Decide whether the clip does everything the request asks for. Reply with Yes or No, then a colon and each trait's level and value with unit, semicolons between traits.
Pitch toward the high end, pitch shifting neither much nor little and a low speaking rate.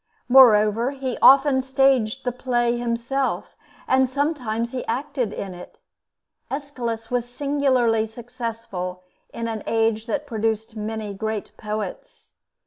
Yes: high, 235 Hz; average, 3.1 semitones; slow, 120 wpm